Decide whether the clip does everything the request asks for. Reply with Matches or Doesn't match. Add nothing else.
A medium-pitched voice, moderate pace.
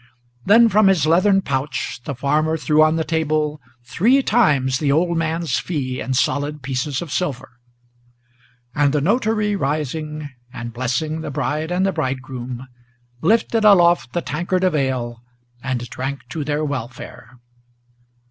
Matches